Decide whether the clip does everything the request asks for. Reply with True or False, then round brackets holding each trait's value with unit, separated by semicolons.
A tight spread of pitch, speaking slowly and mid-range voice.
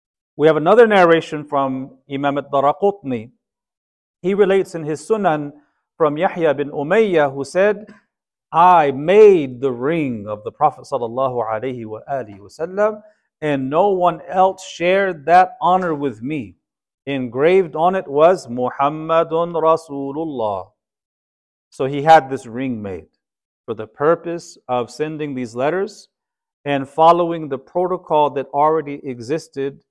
False (4.9 semitones; 120 wpm; 155 Hz)